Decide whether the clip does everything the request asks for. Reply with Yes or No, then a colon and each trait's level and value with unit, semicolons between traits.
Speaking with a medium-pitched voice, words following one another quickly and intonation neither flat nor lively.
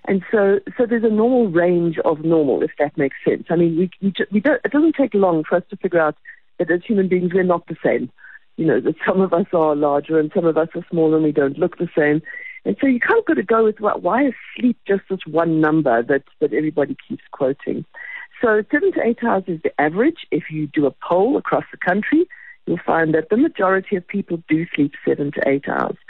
No: medium, 180 Hz; fast, 245 wpm; wide, 5.7 semitones